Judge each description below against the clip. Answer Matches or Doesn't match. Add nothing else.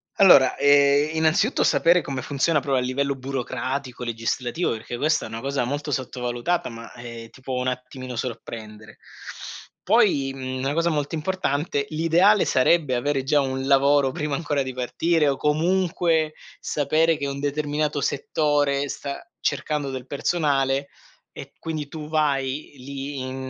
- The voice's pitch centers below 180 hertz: Matches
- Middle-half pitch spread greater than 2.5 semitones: Matches